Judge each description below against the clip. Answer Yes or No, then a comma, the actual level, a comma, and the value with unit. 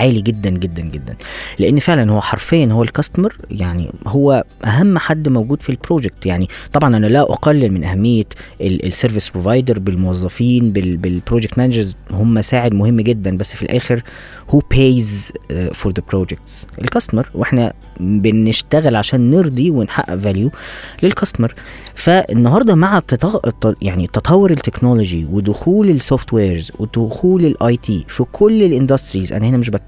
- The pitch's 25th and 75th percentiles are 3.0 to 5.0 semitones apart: No, wide, 5.4 semitones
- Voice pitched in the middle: No, low, 115 Hz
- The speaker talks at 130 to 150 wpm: Yes, fast, 135 wpm